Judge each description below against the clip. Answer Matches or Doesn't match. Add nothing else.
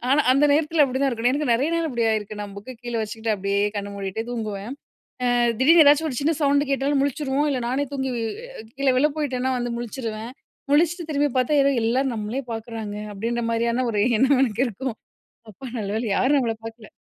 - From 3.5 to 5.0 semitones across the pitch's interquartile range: Matches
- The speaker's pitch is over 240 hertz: Matches